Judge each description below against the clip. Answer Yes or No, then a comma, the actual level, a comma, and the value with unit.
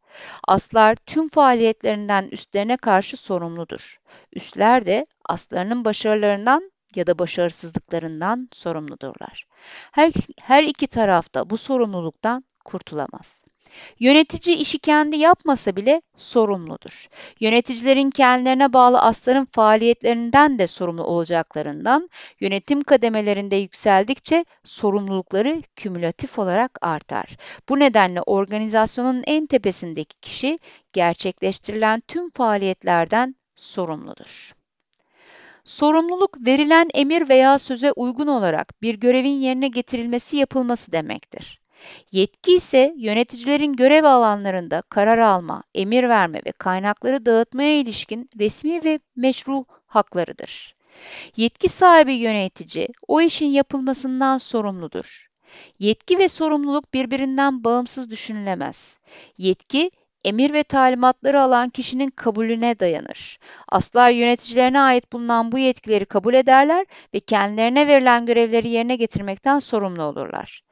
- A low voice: No, high, 240 Hz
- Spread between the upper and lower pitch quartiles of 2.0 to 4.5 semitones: No, average, 5.2 semitones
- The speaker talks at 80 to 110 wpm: Yes, average, 100 wpm